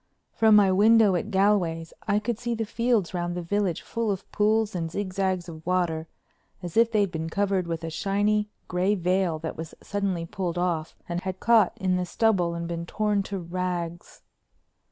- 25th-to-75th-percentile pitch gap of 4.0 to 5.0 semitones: No, average, 3.4 semitones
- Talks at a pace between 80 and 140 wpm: No, average, 185 wpm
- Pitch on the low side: No, medium, 185 Hz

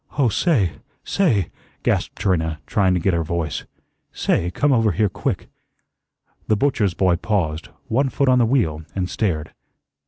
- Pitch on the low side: Yes, very low, 95 Hz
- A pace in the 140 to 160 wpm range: Yes, average, 155 wpm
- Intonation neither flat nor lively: No, wide, 5.8 semitones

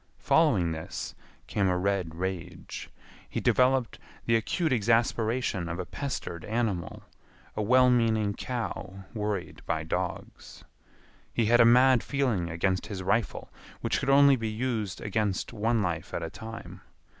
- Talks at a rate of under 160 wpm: Yes, average, 145 wpm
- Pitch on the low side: Yes, low, 110 Hz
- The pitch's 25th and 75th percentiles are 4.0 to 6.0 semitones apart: Yes, average, 4.5 semitones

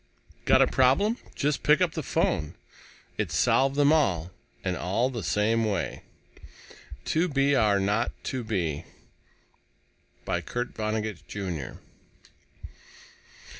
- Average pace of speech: No, slow, 120 wpm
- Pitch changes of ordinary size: No, wide, 5.9 semitones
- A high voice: No, low, 115 Hz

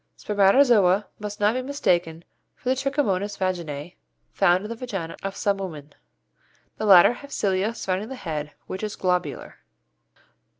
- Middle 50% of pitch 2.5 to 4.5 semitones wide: Yes, average, 3.4 semitones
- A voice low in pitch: No, high, 195 Hz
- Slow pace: No, average, 145 wpm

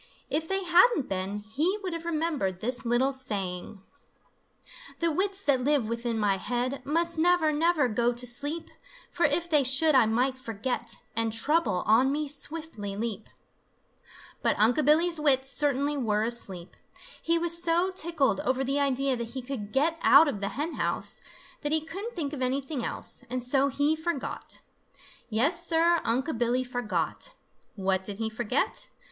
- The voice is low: No, very high, 270 Hz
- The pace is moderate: Yes, average, 165 wpm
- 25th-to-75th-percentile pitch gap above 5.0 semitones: Yes, wide, 5.6 semitones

